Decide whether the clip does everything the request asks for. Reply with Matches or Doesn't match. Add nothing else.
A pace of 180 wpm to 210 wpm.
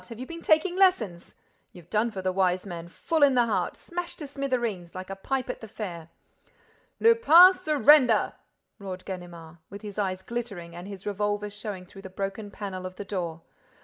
Matches